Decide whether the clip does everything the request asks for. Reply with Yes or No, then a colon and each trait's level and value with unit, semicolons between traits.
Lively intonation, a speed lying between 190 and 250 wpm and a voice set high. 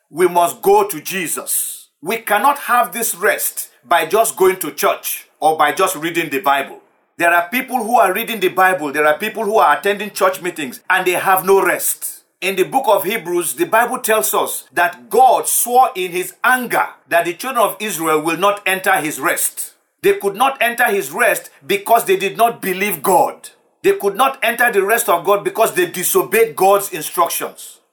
Yes: wide, 5.8 semitones; average, 200 wpm; high, 205 Hz